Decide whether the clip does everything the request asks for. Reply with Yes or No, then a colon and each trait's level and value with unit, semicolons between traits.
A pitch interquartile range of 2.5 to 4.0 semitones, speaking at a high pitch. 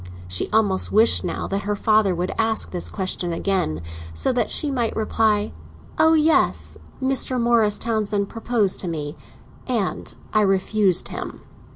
Yes: average, 3.5 semitones; high, 210 Hz